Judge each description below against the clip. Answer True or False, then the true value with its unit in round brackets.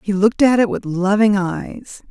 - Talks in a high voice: True (205 Hz)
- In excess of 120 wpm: True (200 wpm)